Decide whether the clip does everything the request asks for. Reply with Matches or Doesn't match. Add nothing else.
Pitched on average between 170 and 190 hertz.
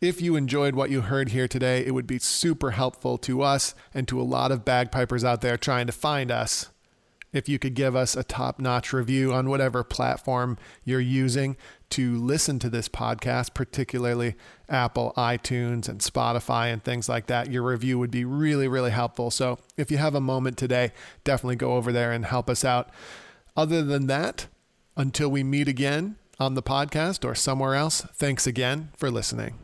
Doesn't match